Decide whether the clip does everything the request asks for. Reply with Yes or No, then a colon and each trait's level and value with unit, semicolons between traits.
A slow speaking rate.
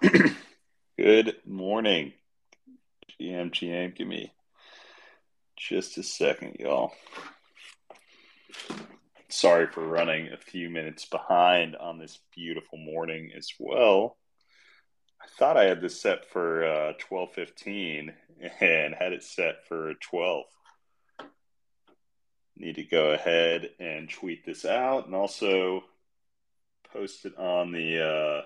Yes: slow, 115 wpm